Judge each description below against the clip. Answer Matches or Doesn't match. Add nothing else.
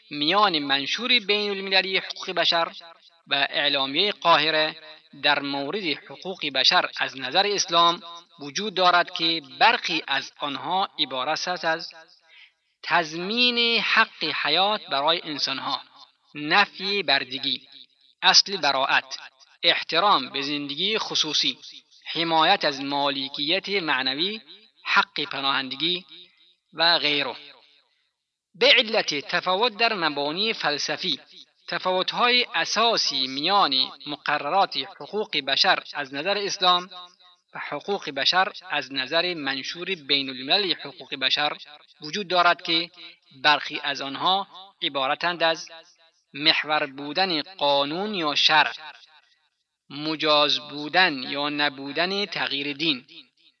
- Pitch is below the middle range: Doesn't match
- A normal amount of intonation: Matches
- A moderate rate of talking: Doesn't match